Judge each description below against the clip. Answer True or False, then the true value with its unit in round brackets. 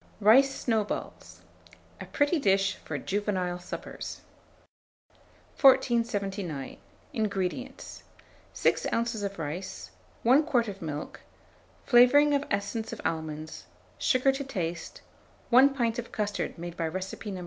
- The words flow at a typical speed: False (115 wpm)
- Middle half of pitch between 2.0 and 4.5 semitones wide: False (5.5 semitones)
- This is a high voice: True (205 Hz)